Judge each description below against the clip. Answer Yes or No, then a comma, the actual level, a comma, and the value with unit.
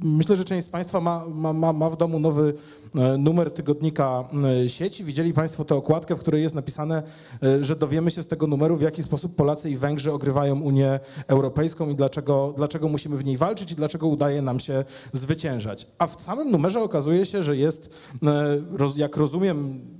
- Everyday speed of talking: No, fast, 180 wpm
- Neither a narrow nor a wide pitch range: No, narrow, 2.3 semitones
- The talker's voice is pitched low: No, medium, 155 Hz